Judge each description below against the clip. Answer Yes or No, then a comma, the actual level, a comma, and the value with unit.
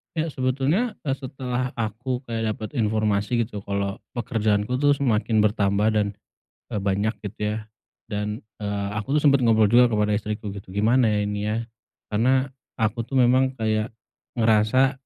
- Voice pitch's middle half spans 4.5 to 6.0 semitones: No, average, 3.2 semitones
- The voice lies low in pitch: Yes, low, 110 Hz